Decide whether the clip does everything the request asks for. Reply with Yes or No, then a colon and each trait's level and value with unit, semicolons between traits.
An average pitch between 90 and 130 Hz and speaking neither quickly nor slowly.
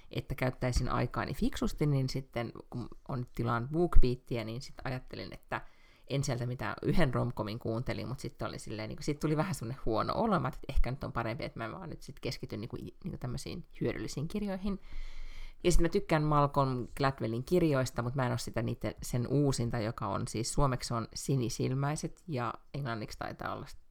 No: low, 125 Hz; fast, 185 wpm